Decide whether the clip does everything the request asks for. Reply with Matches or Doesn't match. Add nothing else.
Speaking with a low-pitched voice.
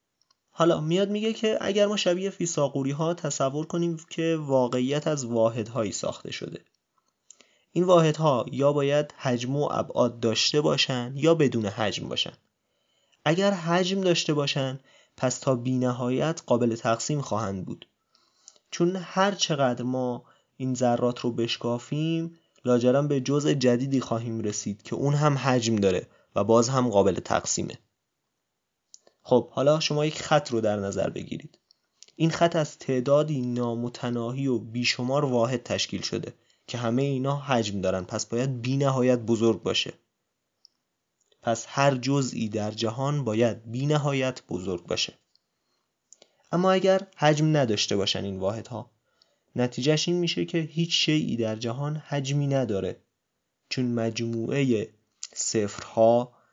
Matches